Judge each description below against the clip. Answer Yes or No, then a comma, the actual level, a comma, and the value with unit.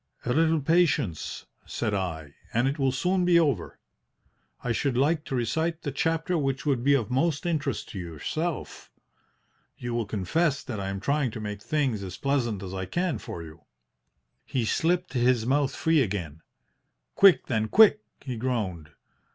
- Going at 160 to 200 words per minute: Yes, average, 165 wpm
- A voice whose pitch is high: No, low, 130 Hz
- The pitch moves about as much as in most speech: No, wide, 7.3 semitones